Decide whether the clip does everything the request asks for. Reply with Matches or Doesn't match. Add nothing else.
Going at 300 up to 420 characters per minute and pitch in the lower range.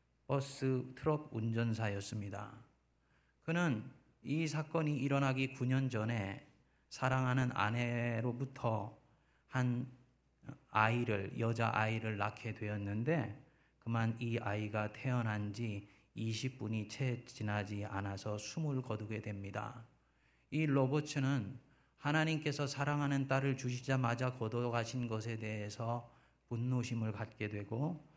Doesn't match